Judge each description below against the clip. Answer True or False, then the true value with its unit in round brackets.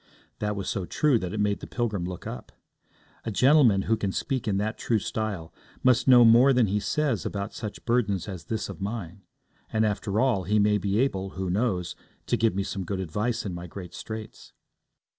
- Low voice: True (105 Hz)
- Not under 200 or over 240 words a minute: True (205 wpm)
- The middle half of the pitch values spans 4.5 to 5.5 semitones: False (3.2 semitones)